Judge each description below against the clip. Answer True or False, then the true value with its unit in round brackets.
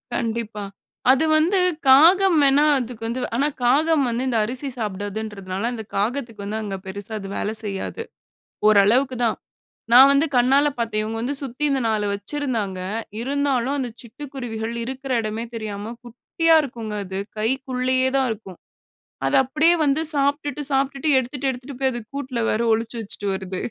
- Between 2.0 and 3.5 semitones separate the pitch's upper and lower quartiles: False (4.3 semitones)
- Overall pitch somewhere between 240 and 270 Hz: True (245 Hz)